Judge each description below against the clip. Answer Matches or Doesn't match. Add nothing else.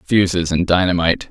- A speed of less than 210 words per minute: Matches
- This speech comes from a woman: Doesn't match